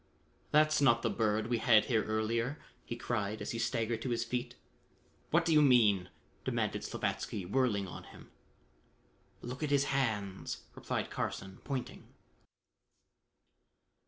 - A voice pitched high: No, low, 115 Hz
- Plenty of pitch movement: No, average, 3.6 semitones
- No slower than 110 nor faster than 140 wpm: Yes, slow, 135 wpm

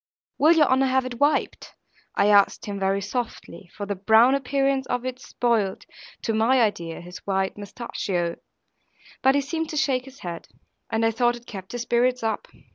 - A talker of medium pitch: No, high, 235 Hz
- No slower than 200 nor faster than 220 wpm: No, average, 185 wpm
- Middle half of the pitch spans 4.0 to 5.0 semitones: Yes, average, 4.7 semitones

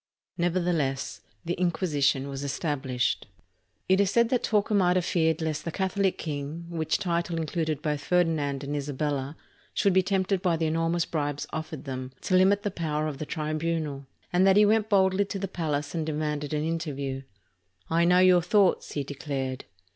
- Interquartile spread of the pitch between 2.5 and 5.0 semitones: Yes, average, 4.0 semitones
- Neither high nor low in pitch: Yes, medium, 160 Hz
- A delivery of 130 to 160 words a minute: No, average, 175 wpm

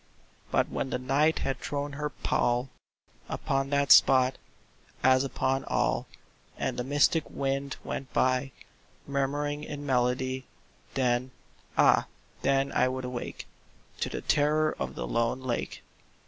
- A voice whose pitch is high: No, low, 135 Hz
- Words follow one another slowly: Yes, slow, 130 wpm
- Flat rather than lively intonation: Yes, narrow, 1.8 semitones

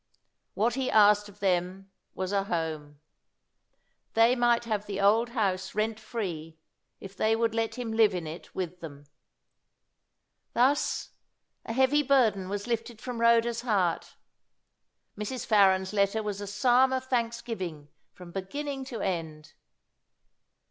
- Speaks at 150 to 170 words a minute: No, slow, 135 wpm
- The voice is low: No, high, 210 Hz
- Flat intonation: No, average, 3.9 semitones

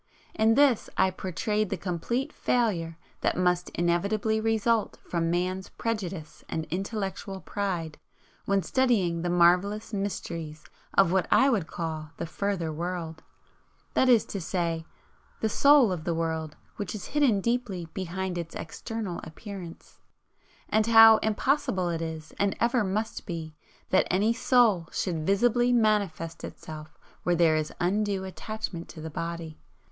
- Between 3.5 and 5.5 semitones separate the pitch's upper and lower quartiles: Yes, average, 4.5 semitones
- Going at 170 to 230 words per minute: No, average, 140 wpm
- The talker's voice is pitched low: No, high, 190 Hz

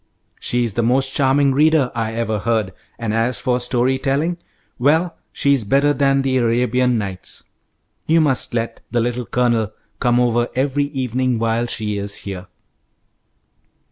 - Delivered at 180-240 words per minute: No, average, 150 wpm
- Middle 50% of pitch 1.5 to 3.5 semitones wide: Yes, average, 2.9 semitones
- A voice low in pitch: Yes, low, 125 Hz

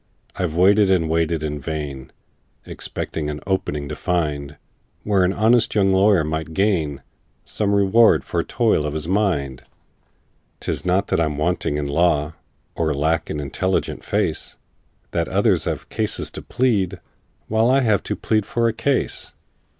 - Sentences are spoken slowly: No, average, 155 wpm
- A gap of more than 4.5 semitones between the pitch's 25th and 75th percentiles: Yes, average, 5.1 semitones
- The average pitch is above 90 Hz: No, very low, 85 Hz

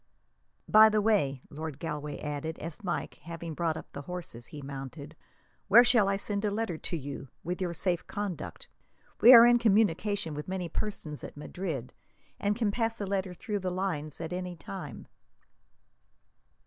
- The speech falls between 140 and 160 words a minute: No, average, 170 wpm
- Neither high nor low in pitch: Yes, medium, 180 Hz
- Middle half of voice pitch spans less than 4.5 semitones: No, average, 5.2 semitones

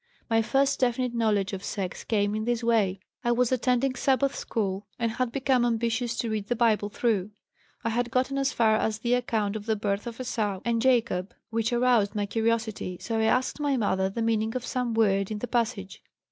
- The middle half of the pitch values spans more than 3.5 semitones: No, average, 2.8 semitones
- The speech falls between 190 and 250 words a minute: Yes, fast, 205 wpm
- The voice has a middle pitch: No, high, 230 Hz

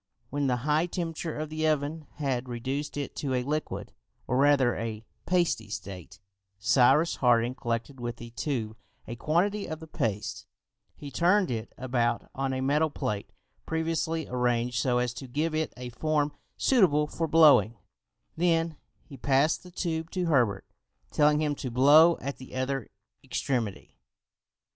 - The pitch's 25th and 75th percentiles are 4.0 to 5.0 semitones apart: Yes, average, 4.4 semitones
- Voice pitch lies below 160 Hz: Yes, medium, 140 Hz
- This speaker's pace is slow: No, average, 155 wpm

